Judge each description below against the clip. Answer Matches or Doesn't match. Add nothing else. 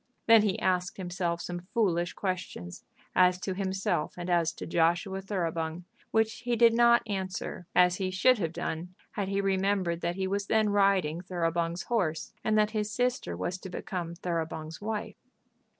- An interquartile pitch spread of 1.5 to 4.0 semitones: Matches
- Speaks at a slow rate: Doesn't match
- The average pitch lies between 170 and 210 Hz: Matches